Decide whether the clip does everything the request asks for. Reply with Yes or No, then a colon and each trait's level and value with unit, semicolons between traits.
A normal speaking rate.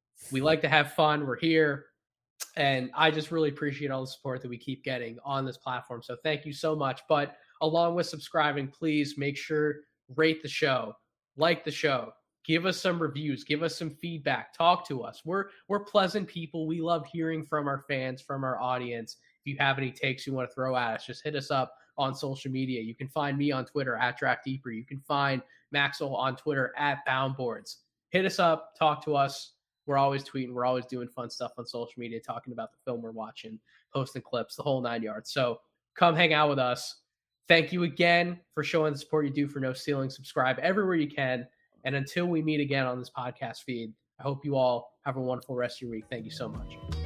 No: fast, 220 wpm